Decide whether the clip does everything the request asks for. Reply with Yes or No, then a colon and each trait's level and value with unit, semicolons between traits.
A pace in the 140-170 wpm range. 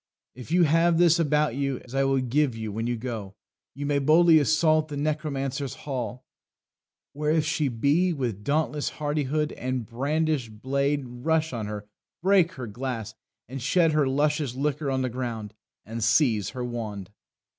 Yes: average, 165 wpm